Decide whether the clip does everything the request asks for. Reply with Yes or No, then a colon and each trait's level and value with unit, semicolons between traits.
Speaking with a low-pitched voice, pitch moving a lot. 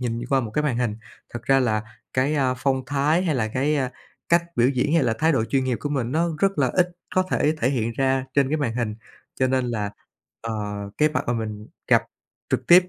No: low, 130 Hz; average, 3.9 semitones